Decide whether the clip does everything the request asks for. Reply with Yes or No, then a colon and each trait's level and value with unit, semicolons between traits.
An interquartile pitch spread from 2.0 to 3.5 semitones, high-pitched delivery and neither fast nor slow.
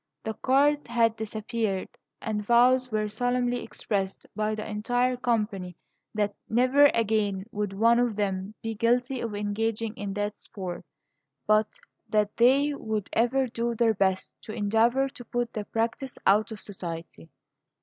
Yes: average, 2.8 semitones; high, 220 Hz; average, 150 wpm